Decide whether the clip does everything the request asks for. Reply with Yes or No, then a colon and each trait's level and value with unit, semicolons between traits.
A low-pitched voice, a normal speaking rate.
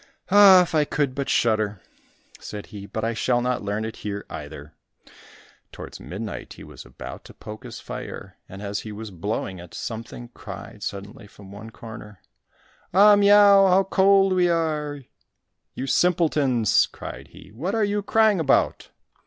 Yes: low, 120 Hz; average, 160 wpm